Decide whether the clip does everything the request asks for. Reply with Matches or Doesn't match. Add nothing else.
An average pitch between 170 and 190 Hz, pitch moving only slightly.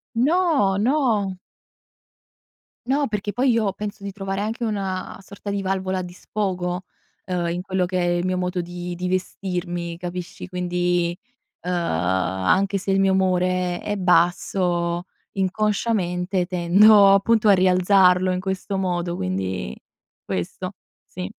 Matches